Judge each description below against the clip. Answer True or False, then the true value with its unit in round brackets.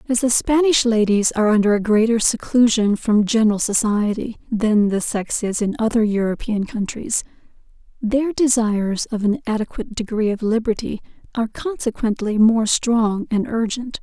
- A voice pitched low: False (220 Hz)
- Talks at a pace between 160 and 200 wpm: False (145 wpm)